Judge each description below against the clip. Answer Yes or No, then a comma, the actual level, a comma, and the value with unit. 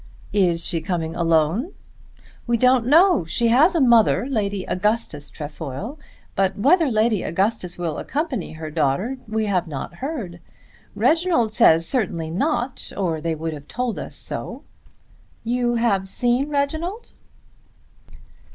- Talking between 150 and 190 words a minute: No, slow, 135 wpm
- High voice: Yes, high, 215 Hz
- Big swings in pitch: Yes, wide, 7.3 semitones